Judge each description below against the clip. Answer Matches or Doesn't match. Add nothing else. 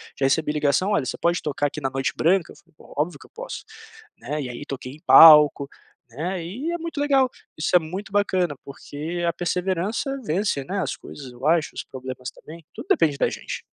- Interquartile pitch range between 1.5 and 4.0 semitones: Doesn't match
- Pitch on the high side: Doesn't match